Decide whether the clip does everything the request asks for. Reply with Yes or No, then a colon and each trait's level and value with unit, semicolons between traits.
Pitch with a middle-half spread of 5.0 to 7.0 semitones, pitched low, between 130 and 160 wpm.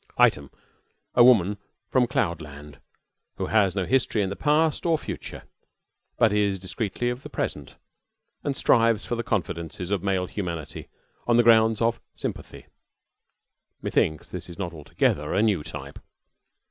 Yes: wide, 5.5 semitones; low, 100 Hz; average, 150 wpm